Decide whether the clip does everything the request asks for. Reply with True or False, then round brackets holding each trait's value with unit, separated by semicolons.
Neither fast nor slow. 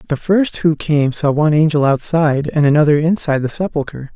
True (190 wpm)